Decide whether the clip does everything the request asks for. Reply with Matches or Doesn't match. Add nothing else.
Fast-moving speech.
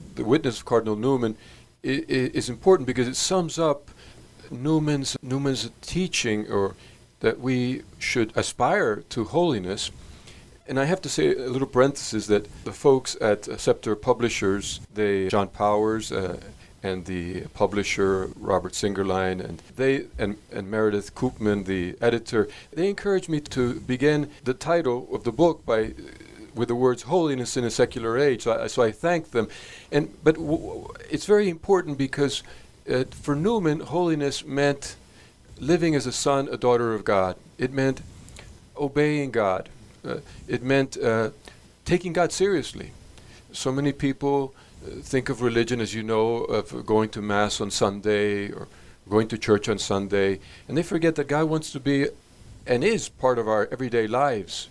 Doesn't match